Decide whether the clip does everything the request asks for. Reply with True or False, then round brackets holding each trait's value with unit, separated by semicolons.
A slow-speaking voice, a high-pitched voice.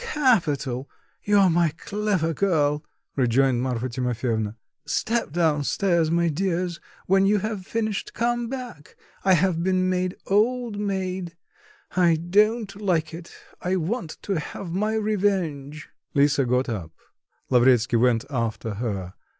False (130 wpm; 170 Hz)